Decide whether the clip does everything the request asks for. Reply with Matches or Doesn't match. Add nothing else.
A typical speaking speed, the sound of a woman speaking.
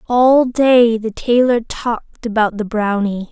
Matches